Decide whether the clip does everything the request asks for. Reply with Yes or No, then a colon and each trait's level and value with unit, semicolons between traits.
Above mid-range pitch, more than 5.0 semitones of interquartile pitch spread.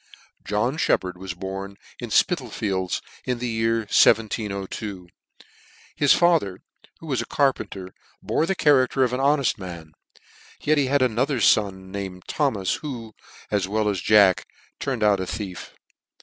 No: low, 105 Hz; wide, 5.4 semitones